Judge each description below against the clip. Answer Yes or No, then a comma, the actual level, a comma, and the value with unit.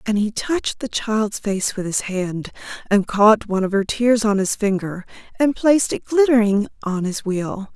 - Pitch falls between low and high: No, high, 210 Hz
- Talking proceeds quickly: No, average, 195 wpm